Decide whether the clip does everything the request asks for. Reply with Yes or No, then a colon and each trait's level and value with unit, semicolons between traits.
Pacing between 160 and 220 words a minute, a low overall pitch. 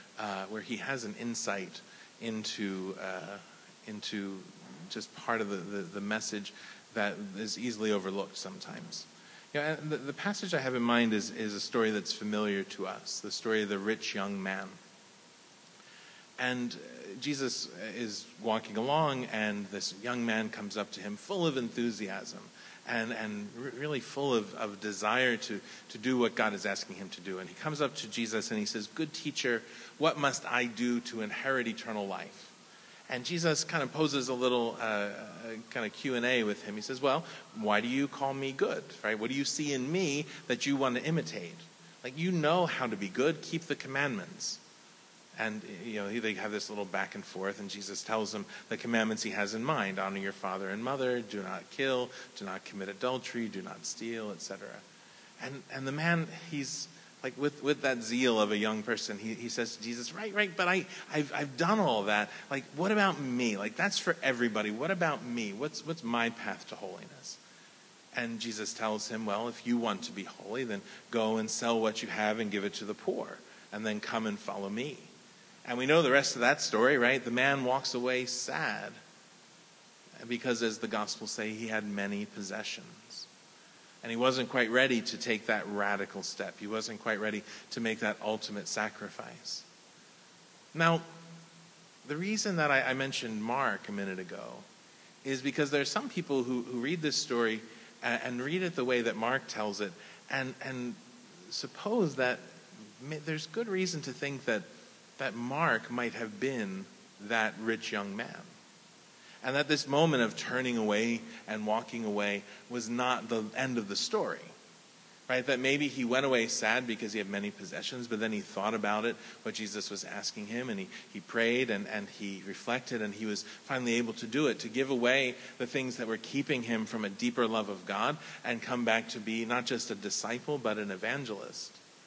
Yes: average, 195 wpm; low, 120 Hz